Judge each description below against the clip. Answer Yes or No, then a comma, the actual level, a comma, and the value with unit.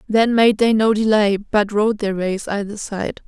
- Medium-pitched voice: No, high, 210 Hz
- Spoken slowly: No, average, 200 wpm